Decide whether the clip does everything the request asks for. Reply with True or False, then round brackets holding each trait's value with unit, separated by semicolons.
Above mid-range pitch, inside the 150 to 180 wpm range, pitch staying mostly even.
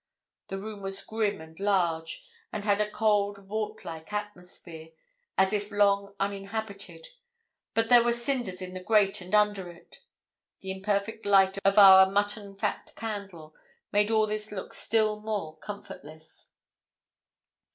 False (200 Hz; 140 wpm; 1.9 semitones)